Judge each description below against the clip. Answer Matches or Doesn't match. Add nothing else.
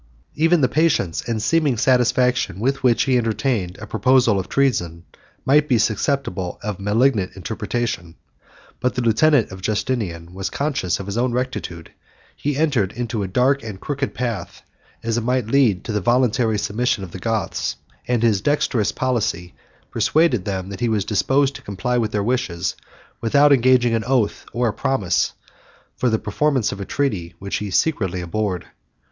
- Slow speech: Doesn't match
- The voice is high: Doesn't match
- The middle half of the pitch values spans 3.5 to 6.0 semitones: Matches